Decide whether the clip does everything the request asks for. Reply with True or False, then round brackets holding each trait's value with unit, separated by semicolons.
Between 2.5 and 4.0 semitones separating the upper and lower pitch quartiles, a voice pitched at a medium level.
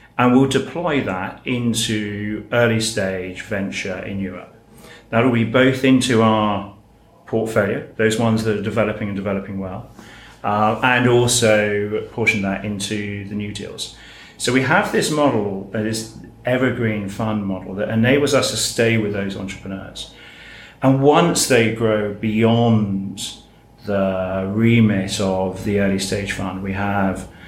False (2.8 semitones; 110 Hz)